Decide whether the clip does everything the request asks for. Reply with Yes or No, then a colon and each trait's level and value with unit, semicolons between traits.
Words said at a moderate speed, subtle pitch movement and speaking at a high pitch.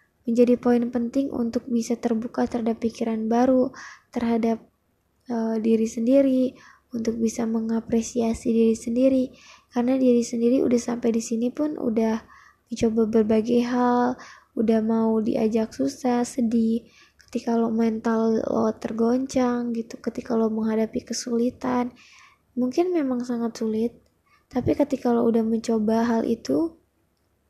Yes: average, 120 wpm; narrow, 1.5 semitones; high, 235 Hz